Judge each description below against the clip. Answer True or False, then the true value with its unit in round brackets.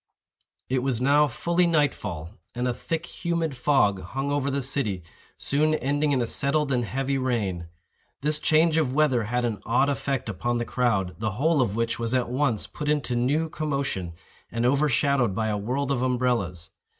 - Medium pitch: False (130 Hz)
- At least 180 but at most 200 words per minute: True (185 wpm)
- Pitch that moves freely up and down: False (3.8 semitones)